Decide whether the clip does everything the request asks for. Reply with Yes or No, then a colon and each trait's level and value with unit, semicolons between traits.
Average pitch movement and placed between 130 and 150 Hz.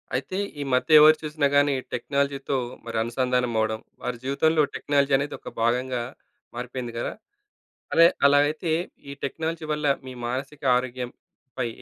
Yes: average, 3.2 semitones; low, 135 Hz